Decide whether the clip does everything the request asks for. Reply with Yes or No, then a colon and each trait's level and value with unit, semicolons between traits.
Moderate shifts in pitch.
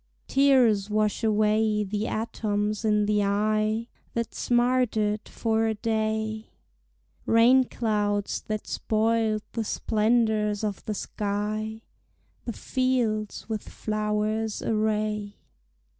No: narrow, 1.1 semitones